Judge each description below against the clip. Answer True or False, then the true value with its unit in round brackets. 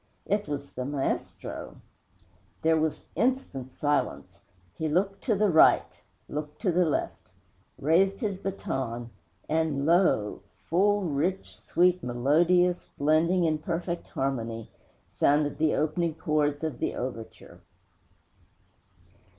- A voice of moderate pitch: True (160 Hz)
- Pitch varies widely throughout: False (4.2 semitones)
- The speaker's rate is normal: False (115 wpm)